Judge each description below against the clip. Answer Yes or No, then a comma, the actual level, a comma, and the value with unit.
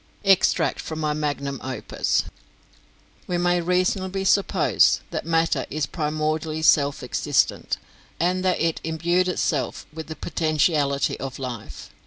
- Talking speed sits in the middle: No, slow, 125 wpm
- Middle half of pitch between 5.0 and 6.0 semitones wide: No, average, 3.4 semitones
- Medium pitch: Yes, medium, 160 Hz